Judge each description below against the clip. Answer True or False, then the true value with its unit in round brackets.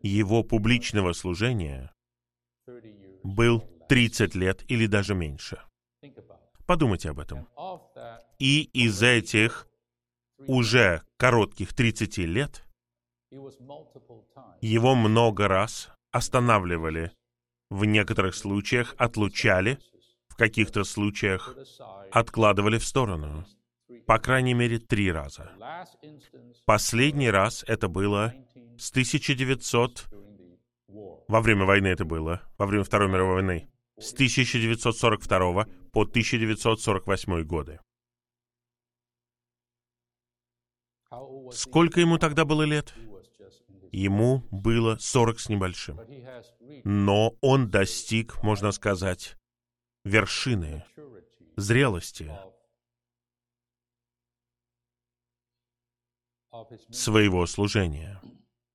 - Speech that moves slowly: True (80 wpm)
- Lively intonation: False (3.4 semitones)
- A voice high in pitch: False (115 Hz)